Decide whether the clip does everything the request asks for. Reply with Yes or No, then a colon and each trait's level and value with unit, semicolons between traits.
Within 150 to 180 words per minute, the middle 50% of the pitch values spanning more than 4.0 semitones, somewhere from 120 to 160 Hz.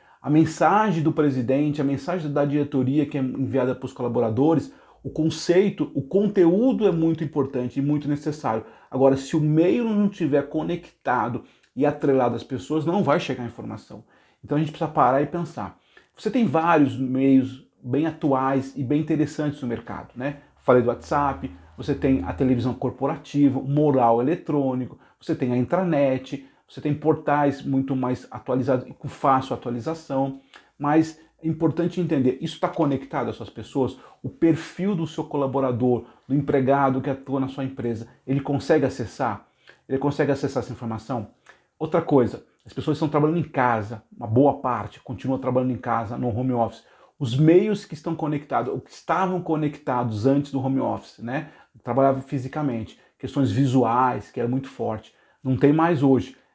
No: average, 165 wpm; average, 3.3 semitones; medium, 140 Hz